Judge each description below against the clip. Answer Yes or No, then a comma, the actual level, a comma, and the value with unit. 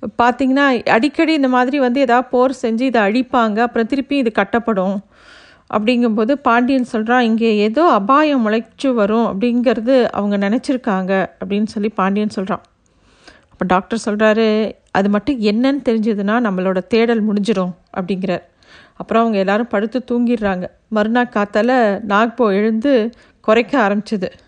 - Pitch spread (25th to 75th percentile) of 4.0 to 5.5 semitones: No, average, 3.3 semitones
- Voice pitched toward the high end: Yes, high, 230 Hz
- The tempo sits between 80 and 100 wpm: No, average, 125 wpm